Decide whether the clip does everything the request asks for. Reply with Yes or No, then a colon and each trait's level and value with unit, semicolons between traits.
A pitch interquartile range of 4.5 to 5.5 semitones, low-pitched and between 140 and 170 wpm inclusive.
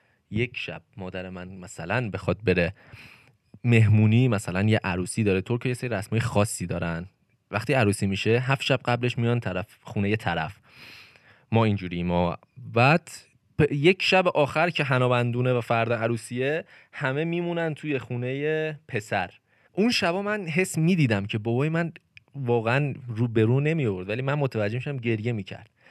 Yes: average, 5.0 semitones; low, 120 Hz; fast, 155 wpm